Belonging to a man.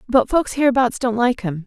No: female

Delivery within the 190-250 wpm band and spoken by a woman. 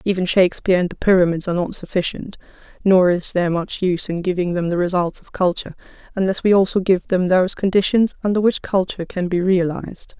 Yes: average, 195 wpm; female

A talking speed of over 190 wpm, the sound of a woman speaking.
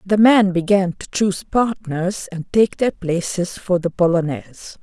No: average, 160 wpm; female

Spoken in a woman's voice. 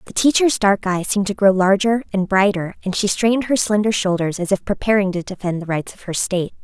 Yes: female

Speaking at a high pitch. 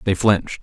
No: very low, 95 Hz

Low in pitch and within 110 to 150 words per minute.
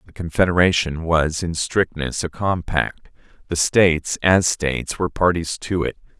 Yes: very low, 85 Hz; average, 145 wpm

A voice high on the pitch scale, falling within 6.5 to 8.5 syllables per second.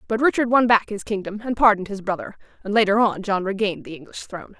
Yes: high, 205 Hz; 6.8 syllables/s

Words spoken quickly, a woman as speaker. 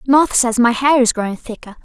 Yes: fast, 230 wpm; female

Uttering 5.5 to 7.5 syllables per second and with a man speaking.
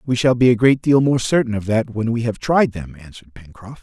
Yes: 5.7 syllables/s; male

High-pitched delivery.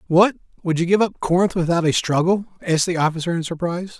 No: medium, 175 Hz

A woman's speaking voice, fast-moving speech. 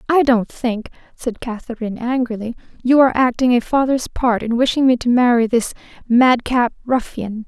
No: female; average, 170 wpm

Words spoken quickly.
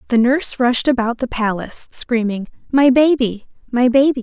No: average, 155 wpm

